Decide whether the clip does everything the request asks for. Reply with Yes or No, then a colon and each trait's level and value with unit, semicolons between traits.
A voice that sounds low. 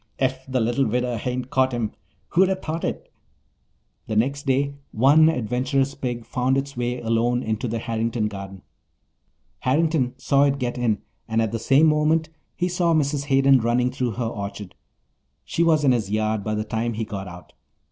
Yes: low, 125 Hz